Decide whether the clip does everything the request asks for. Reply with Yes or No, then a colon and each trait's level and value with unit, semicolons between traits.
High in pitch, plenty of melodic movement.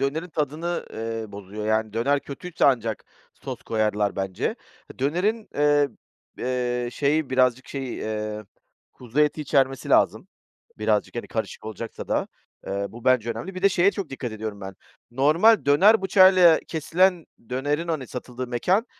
No: low, 130 Hz; wide, 6.2 semitones